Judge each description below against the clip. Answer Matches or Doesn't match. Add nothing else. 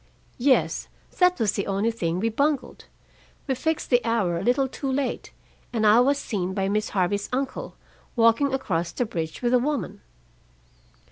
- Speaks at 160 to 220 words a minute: Matches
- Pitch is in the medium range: Doesn't match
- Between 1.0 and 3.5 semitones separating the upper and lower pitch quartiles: Doesn't match